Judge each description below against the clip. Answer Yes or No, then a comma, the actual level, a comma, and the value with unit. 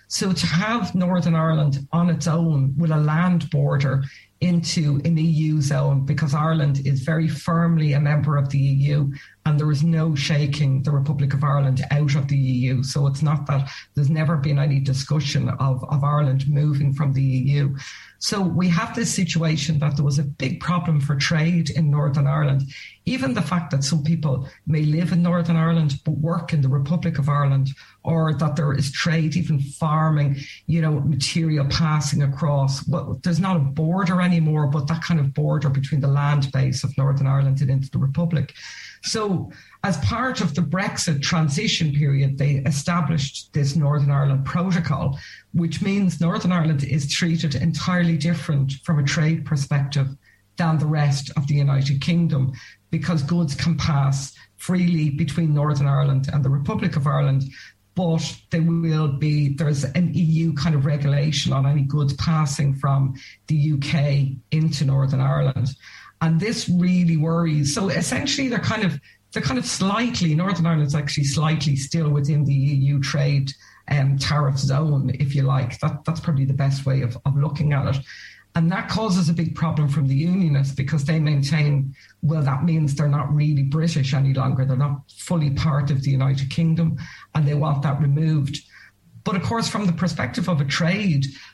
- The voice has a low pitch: No, medium, 150 Hz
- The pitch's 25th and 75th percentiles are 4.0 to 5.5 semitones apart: No, average, 2.8 semitones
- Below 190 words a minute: Yes, average, 180 wpm